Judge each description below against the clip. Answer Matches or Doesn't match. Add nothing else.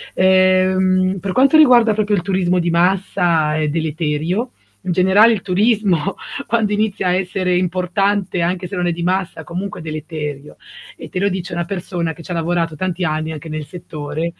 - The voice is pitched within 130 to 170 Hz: Doesn't match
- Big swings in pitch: Doesn't match